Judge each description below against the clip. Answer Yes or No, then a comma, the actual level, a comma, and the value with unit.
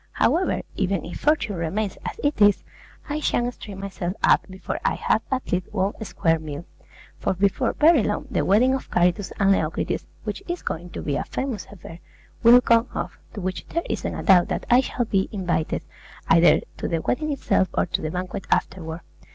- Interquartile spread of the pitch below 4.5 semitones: No, wide, 5.5 semitones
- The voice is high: Yes, high, 195 Hz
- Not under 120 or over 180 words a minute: No, average, 195 wpm